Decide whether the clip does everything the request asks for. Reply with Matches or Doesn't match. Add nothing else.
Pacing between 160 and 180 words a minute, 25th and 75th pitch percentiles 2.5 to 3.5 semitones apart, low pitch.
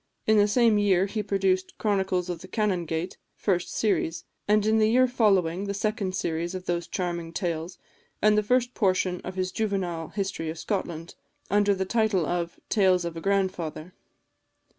Doesn't match